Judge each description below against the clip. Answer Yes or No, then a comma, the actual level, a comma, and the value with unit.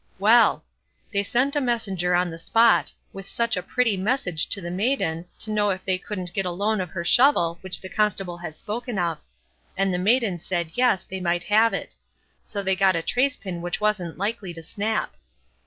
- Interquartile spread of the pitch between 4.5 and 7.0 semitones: No, average, 3.8 semitones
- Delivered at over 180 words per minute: Yes, fast, 205 wpm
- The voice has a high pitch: Yes, high, 195 Hz